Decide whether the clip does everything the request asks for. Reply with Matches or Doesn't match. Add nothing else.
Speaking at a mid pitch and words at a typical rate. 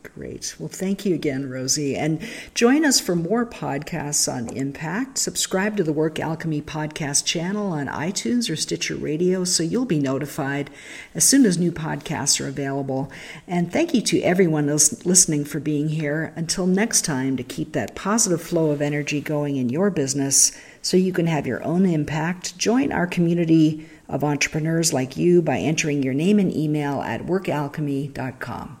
Matches